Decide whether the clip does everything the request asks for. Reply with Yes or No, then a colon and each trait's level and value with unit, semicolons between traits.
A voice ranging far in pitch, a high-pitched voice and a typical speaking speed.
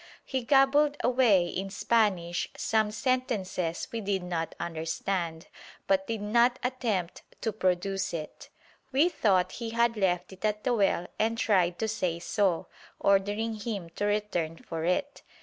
No: average, 4.5 semitones; high, 205 Hz; average, 150 wpm